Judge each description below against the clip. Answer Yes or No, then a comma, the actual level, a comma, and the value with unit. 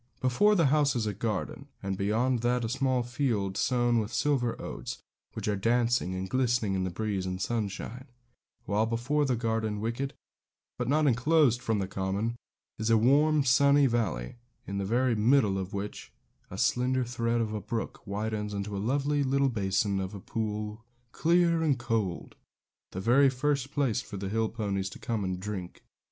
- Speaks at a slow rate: No, average, 175 wpm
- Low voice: Yes, low, 115 Hz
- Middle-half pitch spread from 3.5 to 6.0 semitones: Yes, average, 4.2 semitones